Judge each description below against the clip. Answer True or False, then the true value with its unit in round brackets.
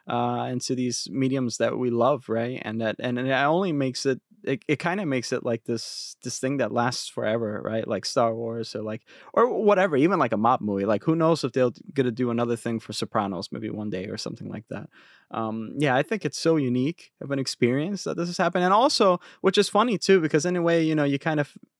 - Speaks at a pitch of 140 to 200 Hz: False (130 Hz)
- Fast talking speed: True (240 wpm)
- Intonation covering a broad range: True (5.8 semitones)